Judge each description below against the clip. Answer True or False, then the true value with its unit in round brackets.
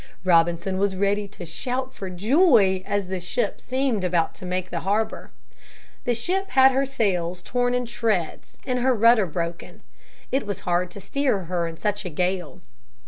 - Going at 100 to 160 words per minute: False (175 wpm)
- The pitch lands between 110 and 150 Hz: False (200 Hz)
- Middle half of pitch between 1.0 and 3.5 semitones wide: False (5.5 semitones)